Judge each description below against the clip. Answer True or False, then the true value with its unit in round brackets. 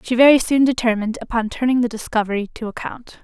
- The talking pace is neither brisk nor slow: True (185 wpm)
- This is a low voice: False (235 Hz)